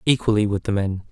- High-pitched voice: No, low, 105 Hz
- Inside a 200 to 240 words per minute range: Yes, fast, 215 wpm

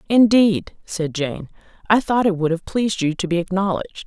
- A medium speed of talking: Yes, average, 190 wpm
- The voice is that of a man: No, female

